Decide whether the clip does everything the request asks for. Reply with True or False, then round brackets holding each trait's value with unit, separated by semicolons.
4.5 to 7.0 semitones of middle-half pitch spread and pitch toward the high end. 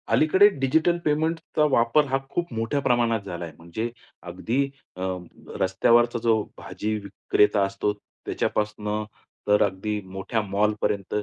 False (4.9 semitones; 110 Hz)